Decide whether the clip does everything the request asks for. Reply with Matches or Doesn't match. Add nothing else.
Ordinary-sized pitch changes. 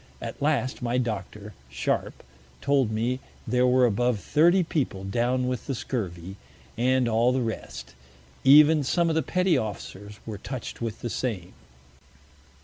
Matches